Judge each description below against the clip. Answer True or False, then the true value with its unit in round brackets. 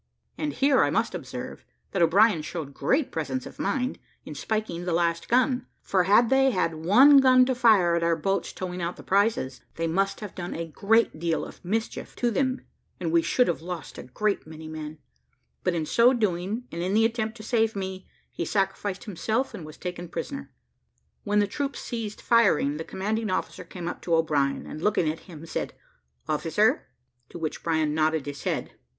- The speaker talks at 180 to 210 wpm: True (195 wpm)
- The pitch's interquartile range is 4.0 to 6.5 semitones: True (5.4 semitones)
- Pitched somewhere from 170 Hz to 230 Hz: True (190 Hz)